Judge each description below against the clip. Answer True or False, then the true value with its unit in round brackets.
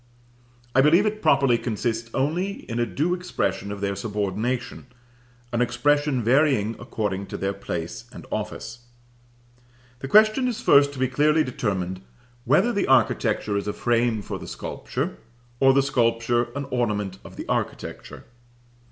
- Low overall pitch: True (120 Hz)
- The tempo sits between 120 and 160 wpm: True (150 wpm)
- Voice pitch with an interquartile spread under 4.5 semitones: False (5.4 semitones)